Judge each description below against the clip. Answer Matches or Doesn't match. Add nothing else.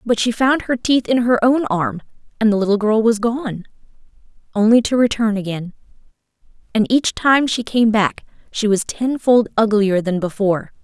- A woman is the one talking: Matches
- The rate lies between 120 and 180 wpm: Matches